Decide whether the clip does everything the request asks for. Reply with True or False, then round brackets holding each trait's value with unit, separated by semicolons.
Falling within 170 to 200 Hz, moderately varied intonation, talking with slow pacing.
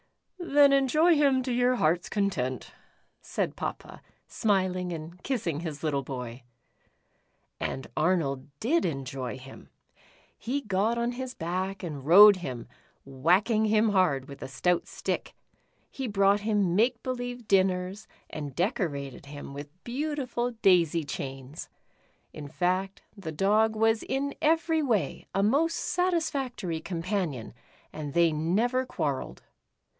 False (190 Hz; 7.8 semitones; 130 wpm)